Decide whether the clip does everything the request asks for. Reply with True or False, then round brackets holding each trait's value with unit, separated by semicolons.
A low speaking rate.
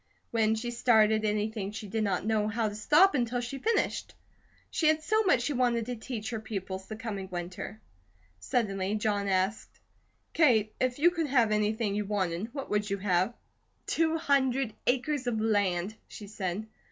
False (175 wpm)